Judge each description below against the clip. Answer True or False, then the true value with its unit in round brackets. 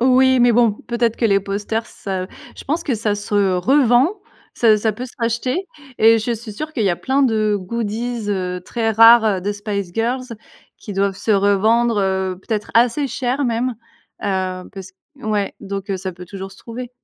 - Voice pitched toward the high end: True (220 Hz)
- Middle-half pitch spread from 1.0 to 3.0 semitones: False (3.4 semitones)